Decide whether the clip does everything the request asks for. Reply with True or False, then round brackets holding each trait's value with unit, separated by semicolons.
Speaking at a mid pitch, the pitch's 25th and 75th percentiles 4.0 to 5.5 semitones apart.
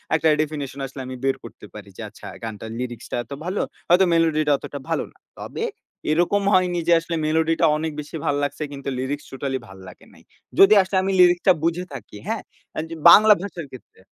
True (155 Hz; 4.4 semitones)